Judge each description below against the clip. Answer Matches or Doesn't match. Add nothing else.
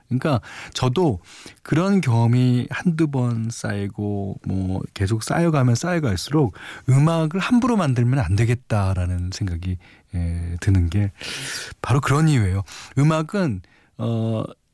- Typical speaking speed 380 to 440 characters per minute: Doesn't match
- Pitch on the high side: Doesn't match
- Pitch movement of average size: Doesn't match